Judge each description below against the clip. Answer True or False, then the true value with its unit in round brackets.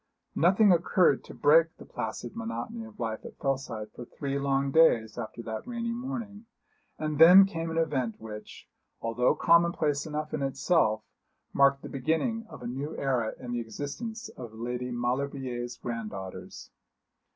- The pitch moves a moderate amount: False (5.9 semitones)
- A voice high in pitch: False (140 Hz)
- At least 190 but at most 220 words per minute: False (150 wpm)